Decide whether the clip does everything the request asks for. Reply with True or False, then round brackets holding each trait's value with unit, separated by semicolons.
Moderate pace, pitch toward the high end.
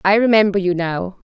True (190 wpm; 195 Hz)